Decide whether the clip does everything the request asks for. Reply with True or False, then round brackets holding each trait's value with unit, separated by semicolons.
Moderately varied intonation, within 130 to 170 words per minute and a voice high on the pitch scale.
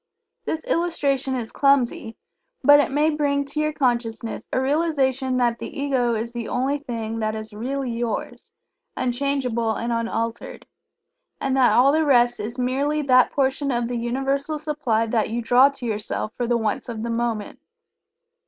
True (3.2 semitones; 165 wpm; 250 Hz)